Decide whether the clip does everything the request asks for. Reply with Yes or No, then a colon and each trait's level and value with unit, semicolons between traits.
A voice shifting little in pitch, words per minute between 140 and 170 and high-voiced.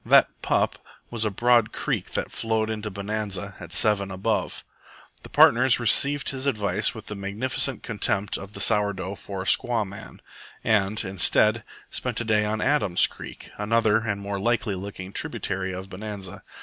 No: narrow, 2.3 semitones; average, 165 wpm; low, 105 Hz